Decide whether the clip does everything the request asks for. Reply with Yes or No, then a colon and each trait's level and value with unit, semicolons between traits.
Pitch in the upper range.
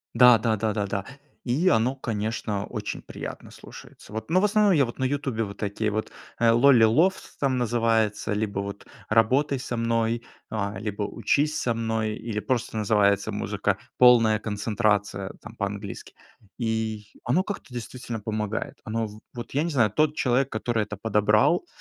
No: low, 115 Hz